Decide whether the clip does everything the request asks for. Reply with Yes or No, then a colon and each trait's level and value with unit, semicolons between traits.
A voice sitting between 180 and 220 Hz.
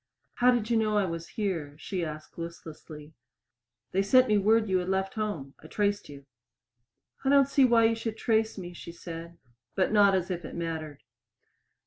Yes: high, 190 Hz